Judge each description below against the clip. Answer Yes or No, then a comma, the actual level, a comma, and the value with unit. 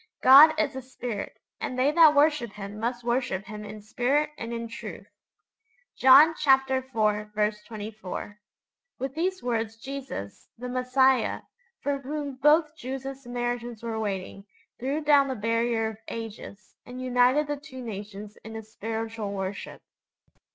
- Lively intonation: No, average, 4.0 semitones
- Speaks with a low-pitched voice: No, high, 240 Hz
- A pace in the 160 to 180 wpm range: No, average, 145 wpm